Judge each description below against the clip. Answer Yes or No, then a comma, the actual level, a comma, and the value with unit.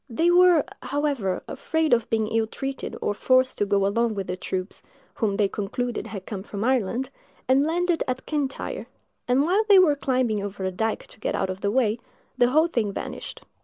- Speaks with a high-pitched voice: Yes, high, 240 Hz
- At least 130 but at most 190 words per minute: No, average, 200 wpm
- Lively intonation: Yes, wide, 5.7 semitones